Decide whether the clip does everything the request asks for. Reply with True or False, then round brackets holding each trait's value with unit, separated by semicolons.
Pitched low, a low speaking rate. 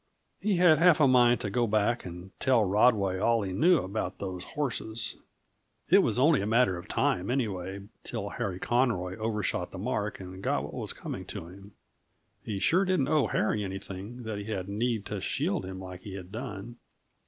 False (105 Hz; 190 wpm)